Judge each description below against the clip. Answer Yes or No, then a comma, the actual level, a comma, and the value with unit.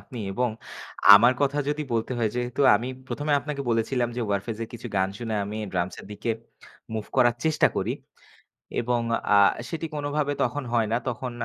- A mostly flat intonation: No, average, 4.1 semitones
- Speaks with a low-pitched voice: Yes, low, 120 Hz